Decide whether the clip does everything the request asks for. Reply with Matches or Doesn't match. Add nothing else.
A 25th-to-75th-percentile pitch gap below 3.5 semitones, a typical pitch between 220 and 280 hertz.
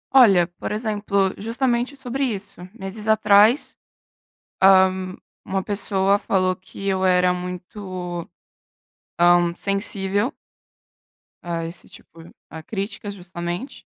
Doesn't match